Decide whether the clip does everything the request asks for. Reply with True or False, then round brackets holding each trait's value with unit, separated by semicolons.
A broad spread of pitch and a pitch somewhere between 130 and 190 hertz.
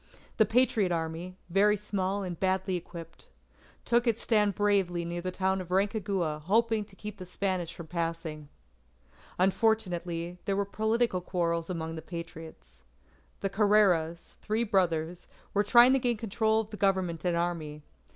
False (3.6 semitones; 185 Hz)